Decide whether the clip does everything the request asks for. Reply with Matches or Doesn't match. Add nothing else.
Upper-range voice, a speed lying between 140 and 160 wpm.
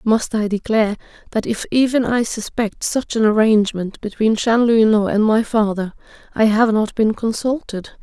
Matches